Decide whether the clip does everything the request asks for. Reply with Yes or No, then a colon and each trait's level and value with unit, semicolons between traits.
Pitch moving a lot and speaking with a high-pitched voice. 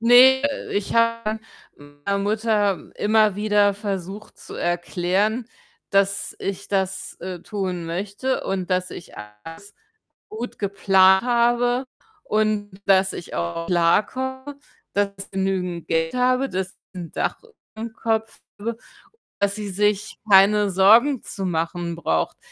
No: average, 3.1 semitones; high, 200 Hz